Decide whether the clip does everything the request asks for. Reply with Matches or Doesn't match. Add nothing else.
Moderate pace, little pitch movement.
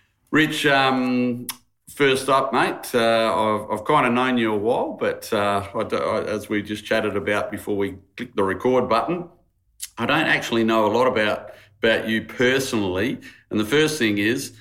Doesn't match